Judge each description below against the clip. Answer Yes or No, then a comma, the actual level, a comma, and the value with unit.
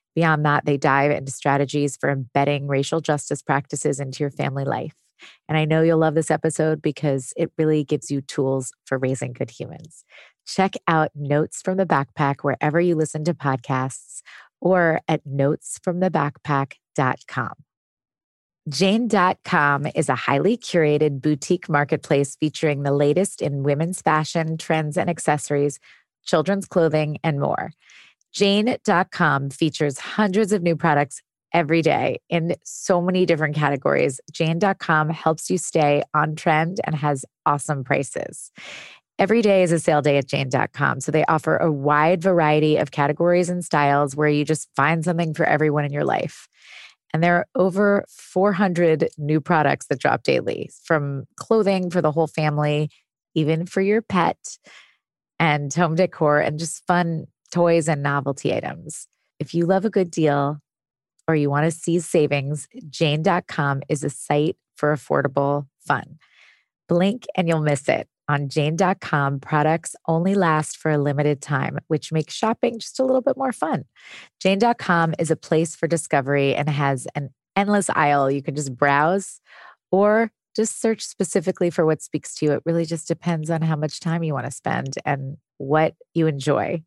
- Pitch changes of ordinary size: Yes, average, 3.2 semitones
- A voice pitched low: No, medium, 155 Hz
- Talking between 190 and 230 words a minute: No, average, 160 wpm